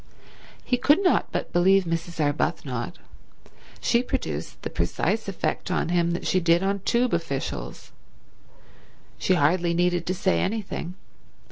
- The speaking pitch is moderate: Yes, medium, 175 Hz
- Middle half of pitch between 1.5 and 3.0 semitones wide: Yes, narrow, 2.6 semitones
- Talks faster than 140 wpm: No, slow, 135 wpm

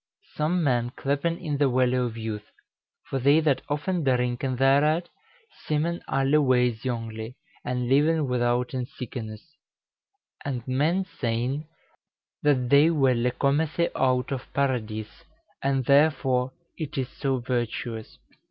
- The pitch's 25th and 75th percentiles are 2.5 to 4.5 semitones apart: Yes, average, 3.1 semitones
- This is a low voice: Yes, low, 130 Hz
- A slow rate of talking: Yes, slow, 125 wpm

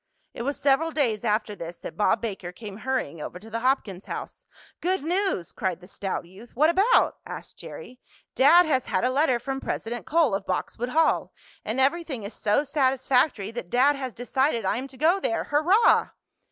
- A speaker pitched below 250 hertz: No, very high, 255 Hz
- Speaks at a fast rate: No, average, 190 wpm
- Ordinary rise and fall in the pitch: No, wide, 5.7 semitones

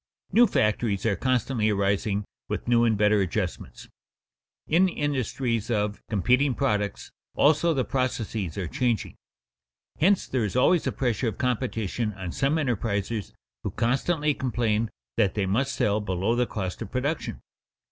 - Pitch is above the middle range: No, low, 115 Hz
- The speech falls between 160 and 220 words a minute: No, average, 145 wpm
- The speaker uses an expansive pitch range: No, average, 4.3 semitones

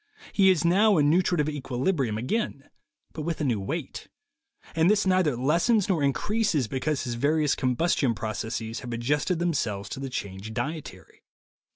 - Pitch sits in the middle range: Yes, medium, 145 Hz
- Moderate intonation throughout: No, wide, 6.1 semitones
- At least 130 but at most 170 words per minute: Yes, average, 160 wpm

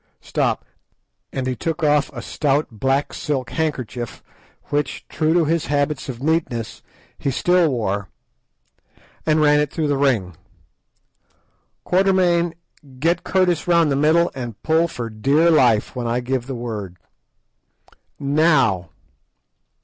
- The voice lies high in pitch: No, medium, 145 Hz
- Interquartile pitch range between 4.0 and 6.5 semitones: Yes, average, 4.7 semitones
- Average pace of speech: No, slow, 130 wpm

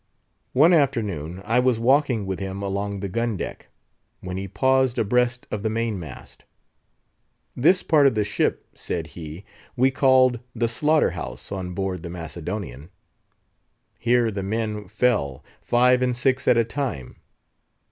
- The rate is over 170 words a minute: No, average, 150 wpm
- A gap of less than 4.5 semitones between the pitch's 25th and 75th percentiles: No, average, 4.8 semitones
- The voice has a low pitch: Yes, low, 110 Hz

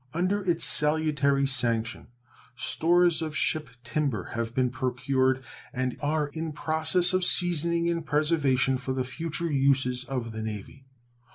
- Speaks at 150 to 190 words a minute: No, slow, 135 wpm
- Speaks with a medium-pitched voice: Yes, medium, 145 Hz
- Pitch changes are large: No, average, 4.0 semitones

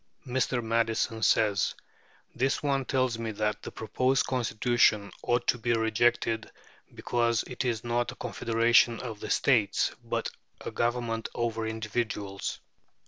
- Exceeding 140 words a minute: No, slow, 135 wpm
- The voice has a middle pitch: No, low, 115 Hz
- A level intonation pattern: Yes, narrow, 1.5 semitones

